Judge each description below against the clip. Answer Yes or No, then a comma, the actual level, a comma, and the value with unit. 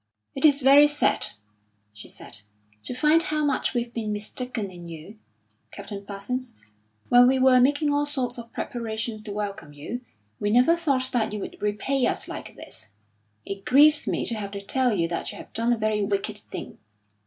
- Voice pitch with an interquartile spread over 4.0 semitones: Yes, average, 4.4 semitones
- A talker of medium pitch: No, high, 235 Hz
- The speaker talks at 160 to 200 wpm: Yes, average, 185 wpm